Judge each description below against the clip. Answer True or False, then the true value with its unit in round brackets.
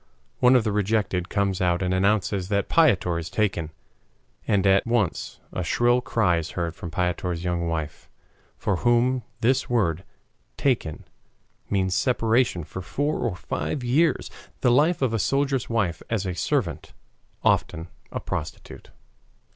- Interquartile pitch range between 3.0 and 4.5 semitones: False (5.5 semitones)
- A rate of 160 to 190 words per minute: False (145 wpm)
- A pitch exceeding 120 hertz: False (100 Hz)